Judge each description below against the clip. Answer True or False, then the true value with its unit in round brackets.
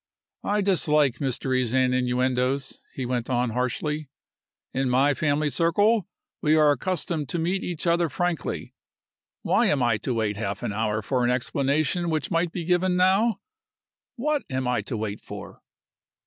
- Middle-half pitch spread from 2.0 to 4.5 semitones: False (5.4 semitones)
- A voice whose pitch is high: False (140 Hz)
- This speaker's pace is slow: False (160 wpm)